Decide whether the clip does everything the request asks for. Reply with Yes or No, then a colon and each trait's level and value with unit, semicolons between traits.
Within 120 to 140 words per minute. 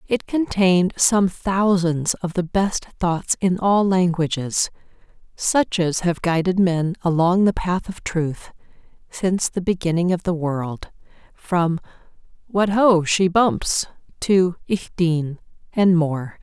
Yes: slow, 135 wpm